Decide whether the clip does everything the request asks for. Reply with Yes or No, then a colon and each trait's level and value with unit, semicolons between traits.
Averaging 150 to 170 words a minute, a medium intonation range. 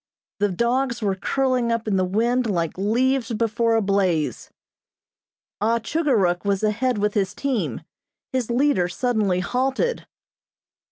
No: slow, 135 wpm; average, 4.2 semitones